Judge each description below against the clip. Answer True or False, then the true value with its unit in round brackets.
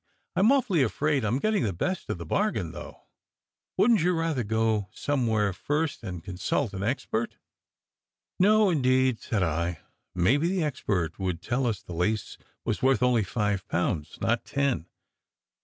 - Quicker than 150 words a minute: True (165 wpm)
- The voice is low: True (115 Hz)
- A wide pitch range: True (7.3 semitones)